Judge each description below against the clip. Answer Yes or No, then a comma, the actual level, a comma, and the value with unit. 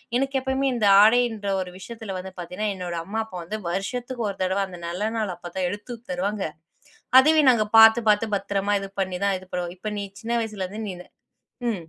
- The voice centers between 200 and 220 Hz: Yes, high, 205 Hz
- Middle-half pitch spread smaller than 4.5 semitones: Yes, average, 3.4 semitones